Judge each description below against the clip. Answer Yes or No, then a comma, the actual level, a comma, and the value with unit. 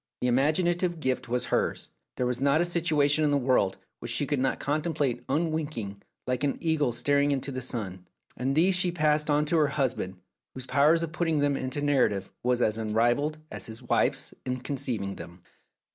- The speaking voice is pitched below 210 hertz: Yes, medium, 140 Hz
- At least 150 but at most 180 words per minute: No, average, 195 wpm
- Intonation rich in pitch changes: No, average, 3.8 semitones